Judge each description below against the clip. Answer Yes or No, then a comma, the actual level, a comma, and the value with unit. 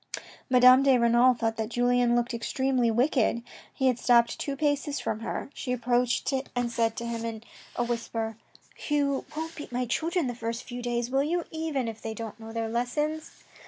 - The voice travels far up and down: No, average, 2.7 semitones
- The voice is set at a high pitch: Yes, high, 245 Hz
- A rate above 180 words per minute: Yes, average, 200 wpm